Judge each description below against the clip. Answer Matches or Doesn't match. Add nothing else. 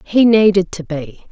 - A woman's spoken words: Matches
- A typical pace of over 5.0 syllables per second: Doesn't match